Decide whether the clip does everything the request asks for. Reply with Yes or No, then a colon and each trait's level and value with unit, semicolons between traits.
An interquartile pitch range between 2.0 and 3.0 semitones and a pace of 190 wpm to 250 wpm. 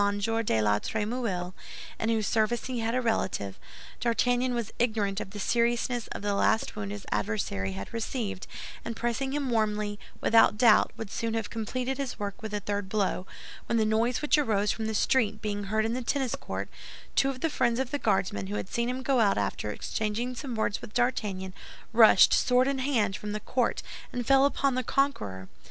No: average, 3.4 semitones; average, 200 wpm